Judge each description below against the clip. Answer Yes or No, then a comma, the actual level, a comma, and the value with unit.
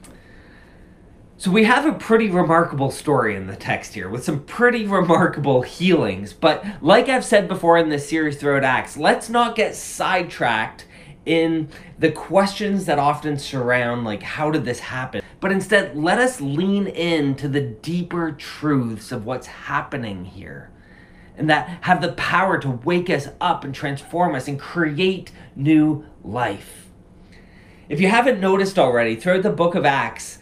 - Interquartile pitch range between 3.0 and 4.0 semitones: No, average, 5.3 semitones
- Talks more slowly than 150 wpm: No, average, 160 wpm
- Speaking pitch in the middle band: Yes, medium, 160 Hz